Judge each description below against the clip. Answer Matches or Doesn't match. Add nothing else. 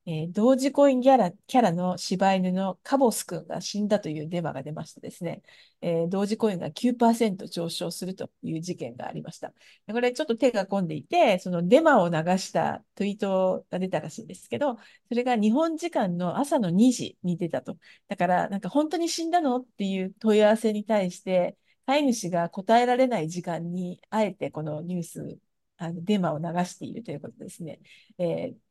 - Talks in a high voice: Matches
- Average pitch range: Doesn't match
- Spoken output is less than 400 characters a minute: Matches